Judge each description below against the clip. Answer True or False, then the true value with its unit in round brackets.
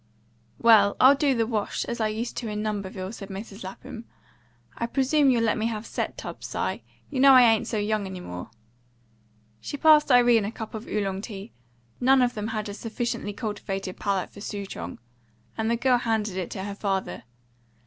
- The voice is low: False (220 Hz)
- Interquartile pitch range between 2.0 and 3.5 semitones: True (3.1 semitones)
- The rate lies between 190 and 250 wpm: True (195 wpm)